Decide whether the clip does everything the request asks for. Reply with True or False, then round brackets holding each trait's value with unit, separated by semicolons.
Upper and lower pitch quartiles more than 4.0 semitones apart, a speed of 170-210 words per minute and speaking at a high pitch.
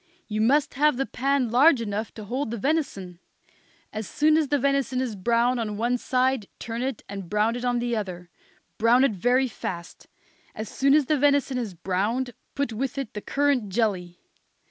True (4.4 semitones; 190 wpm; 240 Hz)